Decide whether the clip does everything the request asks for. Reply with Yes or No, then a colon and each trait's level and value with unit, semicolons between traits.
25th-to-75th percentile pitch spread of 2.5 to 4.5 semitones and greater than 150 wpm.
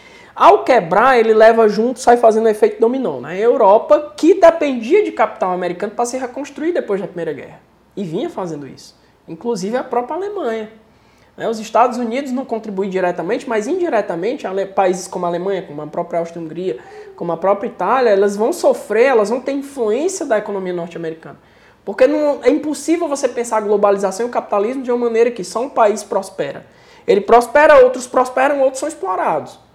No: average, 5.2 semitones; average, 180 wpm